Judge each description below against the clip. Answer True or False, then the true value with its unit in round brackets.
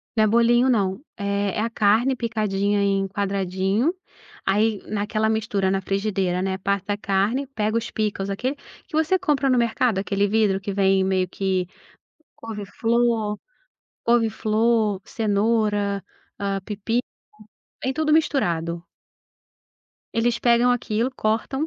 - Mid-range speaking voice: False (215 Hz)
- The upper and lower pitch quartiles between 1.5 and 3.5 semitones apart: True (3.1 semitones)